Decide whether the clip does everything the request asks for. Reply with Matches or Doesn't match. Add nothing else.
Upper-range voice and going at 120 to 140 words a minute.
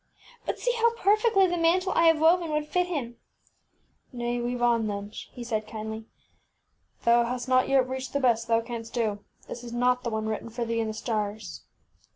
Doesn't match